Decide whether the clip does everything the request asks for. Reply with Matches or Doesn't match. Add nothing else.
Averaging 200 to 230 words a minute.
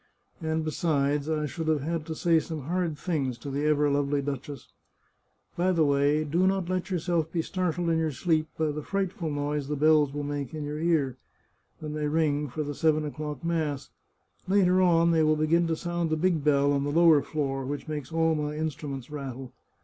Matches